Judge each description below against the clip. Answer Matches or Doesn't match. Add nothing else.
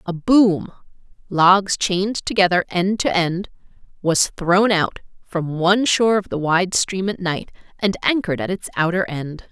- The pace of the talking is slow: Doesn't match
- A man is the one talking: Doesn't match